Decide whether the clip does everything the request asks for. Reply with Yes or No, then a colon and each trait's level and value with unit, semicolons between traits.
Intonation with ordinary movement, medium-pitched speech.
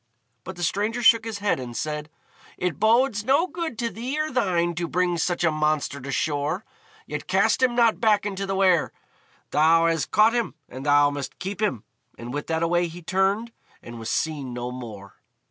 No: wide, 6.7 semitones; medium, 175 Hz